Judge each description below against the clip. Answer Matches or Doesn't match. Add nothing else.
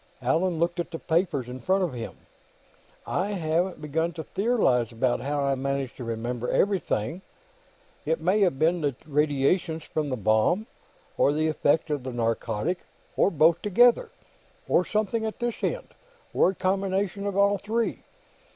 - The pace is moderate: Matches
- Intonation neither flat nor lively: Doesn't match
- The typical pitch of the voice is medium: Matches